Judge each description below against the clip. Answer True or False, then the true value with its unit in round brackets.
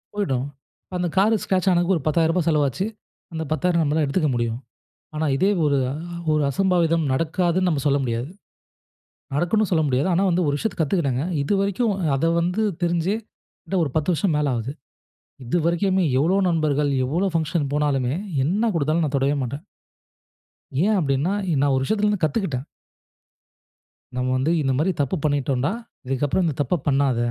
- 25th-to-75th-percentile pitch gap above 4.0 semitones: True (4.5 semitones)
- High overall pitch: False (155 Hz)